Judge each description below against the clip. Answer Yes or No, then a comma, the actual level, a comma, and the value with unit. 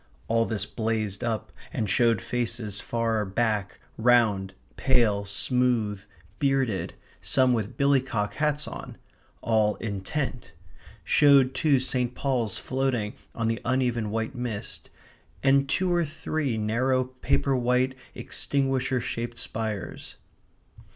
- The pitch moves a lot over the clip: No, average, 3.3 semitones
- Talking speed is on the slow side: Yes, slow, 115 wpm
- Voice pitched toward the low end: Yes, low, 120 Hz